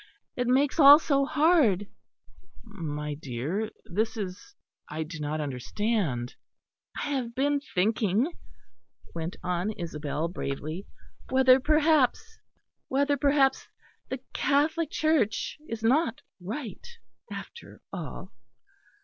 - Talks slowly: Yes, slow, 100 wpm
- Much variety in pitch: Yes, wide, 8.7 semitones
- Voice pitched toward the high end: Yes, high, 225 Hz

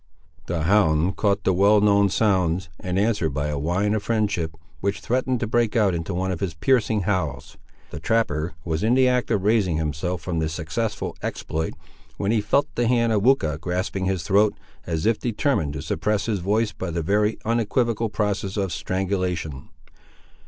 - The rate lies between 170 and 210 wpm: Yes, average, 180 wpm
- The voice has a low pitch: Yes, low, 100 Hz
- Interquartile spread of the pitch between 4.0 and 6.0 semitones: Yes, average, 4.4 semitones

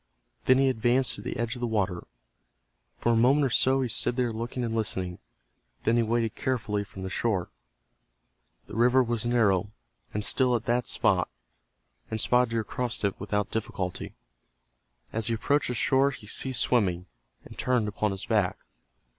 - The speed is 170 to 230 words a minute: Yes, average, 175 wpm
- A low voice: Yes, low, 115 Hz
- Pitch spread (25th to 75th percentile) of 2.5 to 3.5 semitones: Yes, average, 3.1 semitones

